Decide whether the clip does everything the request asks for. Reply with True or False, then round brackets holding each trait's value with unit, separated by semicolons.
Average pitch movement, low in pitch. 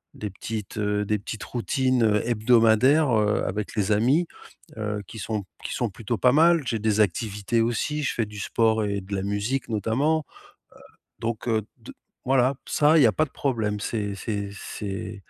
True (3.1 semitones; 110 Hz)